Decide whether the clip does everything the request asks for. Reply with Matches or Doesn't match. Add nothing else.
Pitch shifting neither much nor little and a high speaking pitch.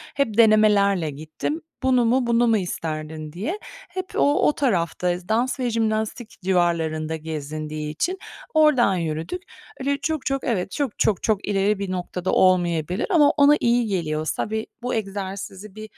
Doesn't match